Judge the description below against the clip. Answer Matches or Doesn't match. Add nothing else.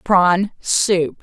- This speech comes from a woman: Matches